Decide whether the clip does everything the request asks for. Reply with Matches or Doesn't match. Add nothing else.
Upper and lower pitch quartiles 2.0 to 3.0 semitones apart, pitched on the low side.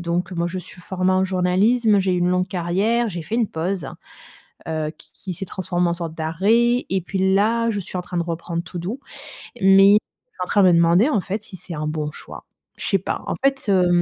Doesn't match